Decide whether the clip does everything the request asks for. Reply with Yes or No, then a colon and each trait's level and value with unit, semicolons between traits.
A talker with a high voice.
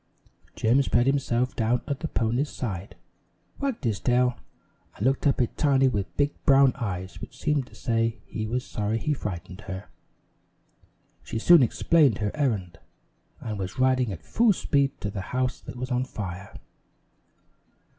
No: low, 125 Hz